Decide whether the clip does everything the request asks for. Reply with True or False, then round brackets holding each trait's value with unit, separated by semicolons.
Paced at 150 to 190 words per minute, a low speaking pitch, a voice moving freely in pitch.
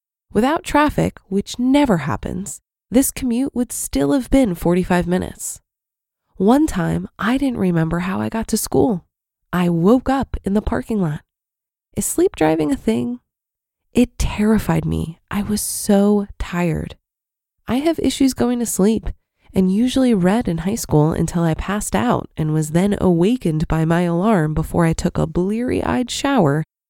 False (160 wpm; 200 Hz; 6.1 semitones)